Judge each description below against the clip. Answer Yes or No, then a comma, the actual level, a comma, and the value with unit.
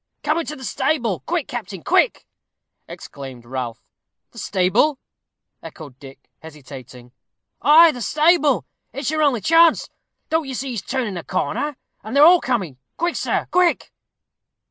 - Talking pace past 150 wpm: No, average, 145 wpm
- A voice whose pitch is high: Yes, very high, 250 Hz